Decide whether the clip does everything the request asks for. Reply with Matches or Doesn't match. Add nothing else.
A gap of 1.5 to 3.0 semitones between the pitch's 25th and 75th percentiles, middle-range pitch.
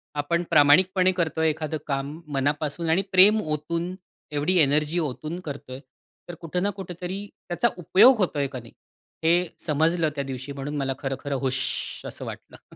Doesn't match